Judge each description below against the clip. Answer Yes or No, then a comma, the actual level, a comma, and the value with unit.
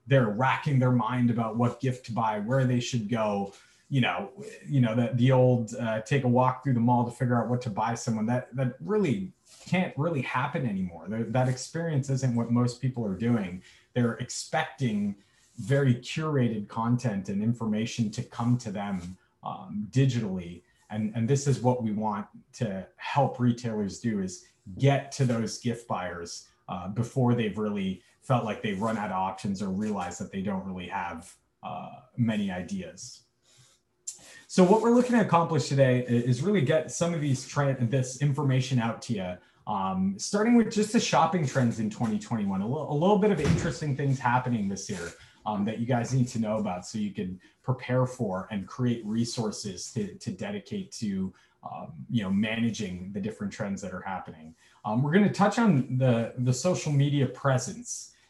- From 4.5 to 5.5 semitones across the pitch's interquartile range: No, average, 4.1 semitones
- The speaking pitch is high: No, low, 125 Hz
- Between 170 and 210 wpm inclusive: Yes, average, 185 wpm